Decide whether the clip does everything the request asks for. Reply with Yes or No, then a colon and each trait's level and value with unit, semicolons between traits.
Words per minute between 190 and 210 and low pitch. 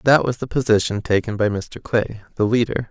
Yes: fast, 205 wpm; low, 110 Hz